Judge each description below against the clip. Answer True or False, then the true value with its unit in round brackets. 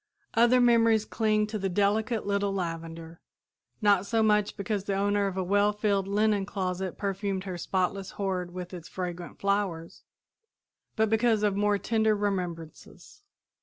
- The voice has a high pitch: True (200 Hz)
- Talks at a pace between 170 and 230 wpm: False (150 wpm)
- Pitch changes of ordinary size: False (2.3 semitones)